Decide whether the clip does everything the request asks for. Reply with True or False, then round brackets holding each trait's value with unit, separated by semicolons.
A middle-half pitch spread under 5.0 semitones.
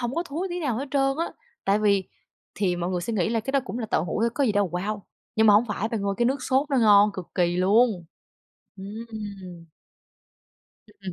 True (4.4 semitones)